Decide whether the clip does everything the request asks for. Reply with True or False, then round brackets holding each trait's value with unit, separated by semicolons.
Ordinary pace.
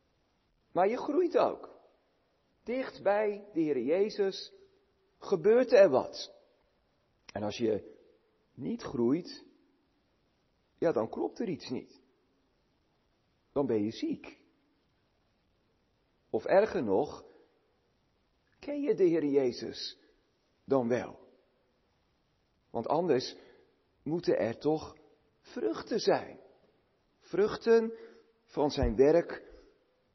False (95 wpm)